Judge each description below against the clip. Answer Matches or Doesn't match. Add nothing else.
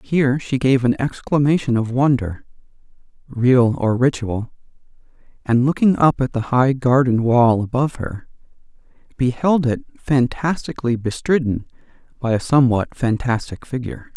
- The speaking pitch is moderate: Doesn't match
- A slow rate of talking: Matches